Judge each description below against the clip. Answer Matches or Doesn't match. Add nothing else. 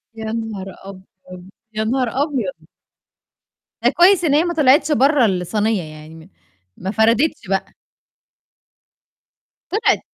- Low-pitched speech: Doesn't match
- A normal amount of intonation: Doesn't match